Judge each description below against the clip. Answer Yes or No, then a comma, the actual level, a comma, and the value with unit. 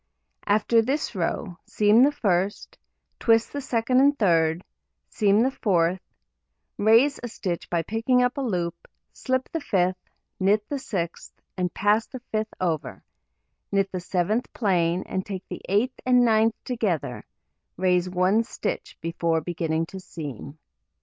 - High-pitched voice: Yes, high, 200 Hz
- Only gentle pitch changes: No, average, 5.0 semitones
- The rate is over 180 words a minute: No, average, 145 wpm